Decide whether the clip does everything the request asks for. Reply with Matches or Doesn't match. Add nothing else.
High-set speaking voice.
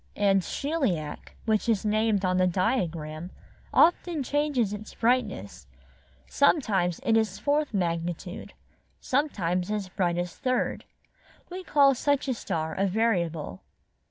Matches